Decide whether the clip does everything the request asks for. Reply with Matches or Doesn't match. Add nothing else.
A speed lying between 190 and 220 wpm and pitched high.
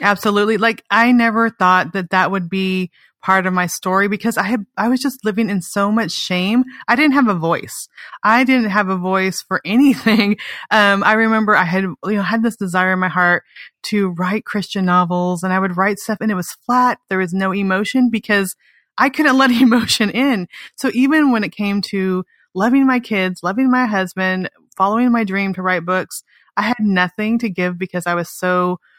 Matches